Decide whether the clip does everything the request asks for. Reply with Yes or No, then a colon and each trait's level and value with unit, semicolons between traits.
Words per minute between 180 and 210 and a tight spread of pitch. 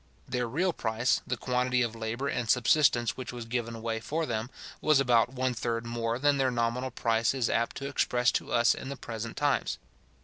Yes: average, 200 wpm; narrow, 2.0 semitones